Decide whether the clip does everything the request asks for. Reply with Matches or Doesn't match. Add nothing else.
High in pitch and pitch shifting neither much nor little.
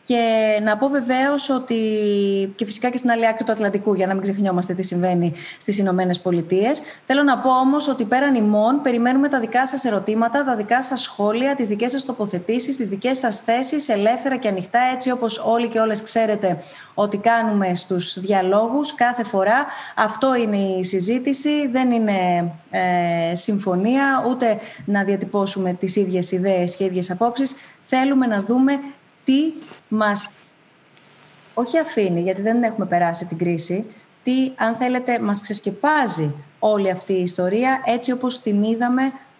Matches